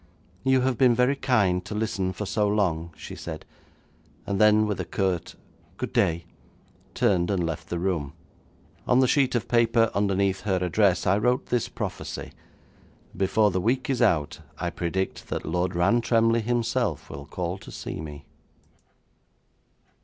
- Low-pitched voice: Yes, low, 100 Hz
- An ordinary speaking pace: Yes, average, 155 wpm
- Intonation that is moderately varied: Yes, average, 4.6 semitones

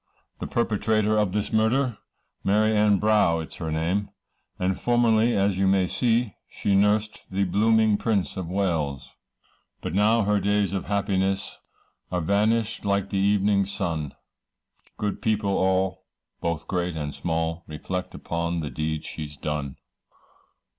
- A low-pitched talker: Yes, low, 100 Hz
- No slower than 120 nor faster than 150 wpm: Yes, average, 145 wpm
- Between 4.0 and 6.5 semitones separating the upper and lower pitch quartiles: No, average, 3.6 semitones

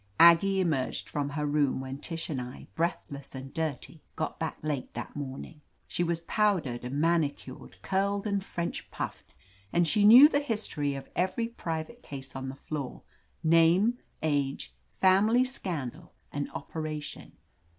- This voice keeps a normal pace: Yes, average, 150 wpm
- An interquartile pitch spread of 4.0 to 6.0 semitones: Yes, average, 5.2 semitones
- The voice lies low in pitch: No, medium, 160 Hz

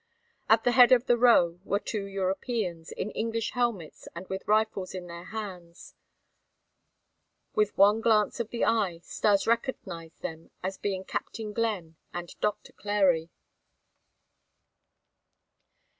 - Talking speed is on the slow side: Yes, slow, 130 wpm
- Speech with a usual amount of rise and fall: Yes, average, 4.0 semitones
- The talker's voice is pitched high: Yes, high, 200 Hz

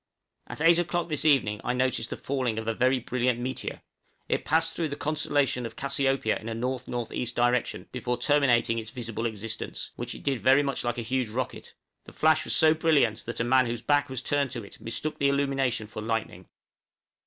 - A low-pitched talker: Yes, low, 125 Hz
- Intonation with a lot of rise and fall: No, average, 3.3 semitones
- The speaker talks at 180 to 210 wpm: Yes, average, 200 wpm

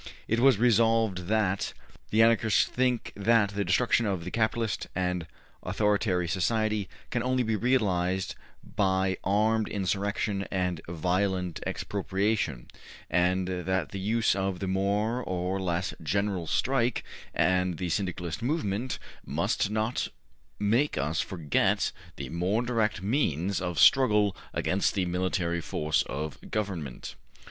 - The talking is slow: Yes, slow, 130 wpm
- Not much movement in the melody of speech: No, average, 3.5 semitones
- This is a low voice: Yes, low, 100 Hz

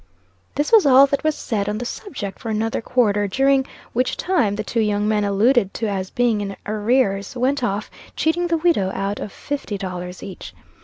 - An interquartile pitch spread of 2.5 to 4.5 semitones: No, average, 5.0 semitones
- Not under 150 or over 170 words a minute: No, average, 195 wpm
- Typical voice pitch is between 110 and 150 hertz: No, high, 220 Hz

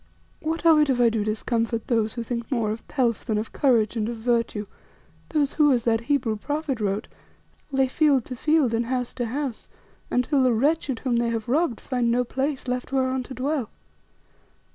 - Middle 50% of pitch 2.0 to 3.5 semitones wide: Yes, average, 3.1 semitones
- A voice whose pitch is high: Yes, high, 245 Hz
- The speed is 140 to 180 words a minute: No, average, 195 wpm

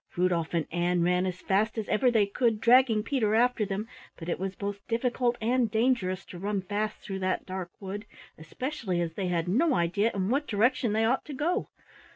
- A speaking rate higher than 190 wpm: Yes, average, 200 wpm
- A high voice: Yes, high, 210 Hz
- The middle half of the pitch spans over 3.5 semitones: Yes, average, 4.5 semitones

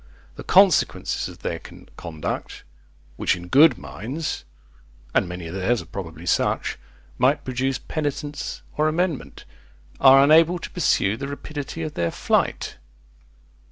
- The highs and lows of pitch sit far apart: Yes, wide, 8.8 semitones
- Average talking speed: No, slow, 130 wpm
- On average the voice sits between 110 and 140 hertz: Yes, low, 135 Hz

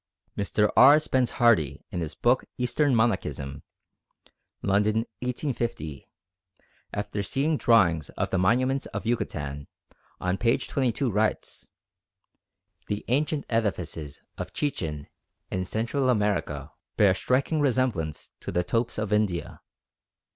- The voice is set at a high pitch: No, low, 110 Hz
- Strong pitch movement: Yes, wide, 5.7 semitones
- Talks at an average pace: No, slow, 120 wpm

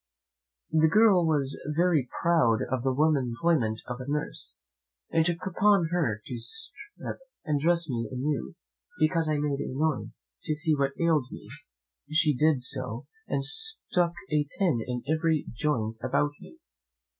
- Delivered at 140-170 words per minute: Yes, average, 155 wpm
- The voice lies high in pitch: No, medium, 150 Hz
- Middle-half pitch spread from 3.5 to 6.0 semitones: Yes, average, 4.4 semitones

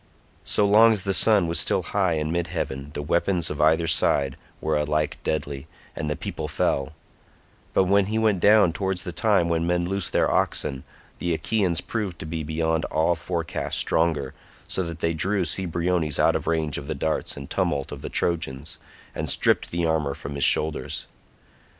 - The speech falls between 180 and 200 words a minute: Yes, average, 185 wpm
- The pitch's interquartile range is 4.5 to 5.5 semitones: No, average, 3.3 semitones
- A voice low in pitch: Yes, very low, 85 Hz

